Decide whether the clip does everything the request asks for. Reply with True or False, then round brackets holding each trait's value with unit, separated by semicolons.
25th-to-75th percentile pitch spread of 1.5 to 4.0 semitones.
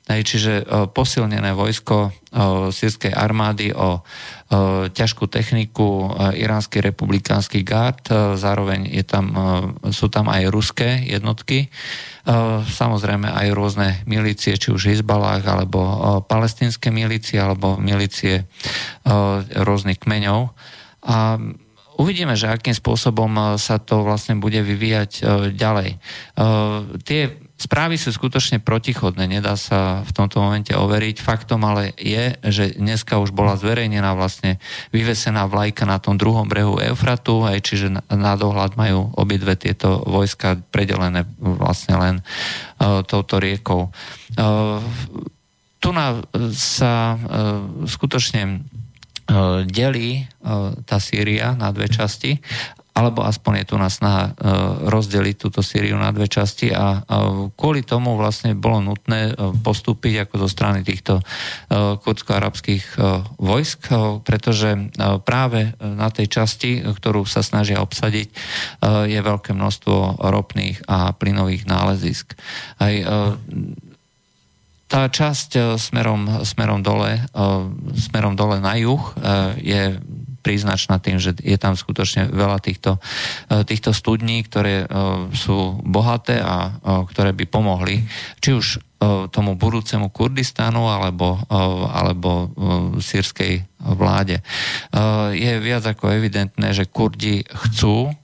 True (2.5 semitones)